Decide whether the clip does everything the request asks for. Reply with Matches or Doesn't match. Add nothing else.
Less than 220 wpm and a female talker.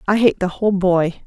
Doesn't match